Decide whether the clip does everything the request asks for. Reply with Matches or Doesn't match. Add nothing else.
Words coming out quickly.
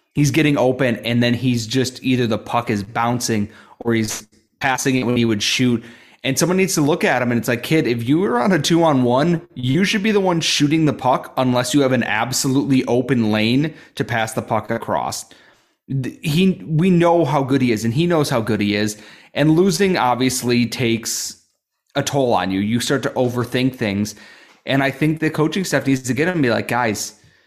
Matches